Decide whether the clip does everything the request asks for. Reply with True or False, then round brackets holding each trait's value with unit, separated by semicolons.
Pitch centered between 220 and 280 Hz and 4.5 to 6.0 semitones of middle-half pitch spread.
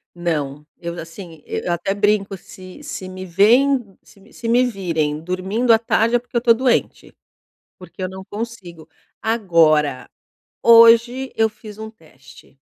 False (200 Hz; 5.0 semitones)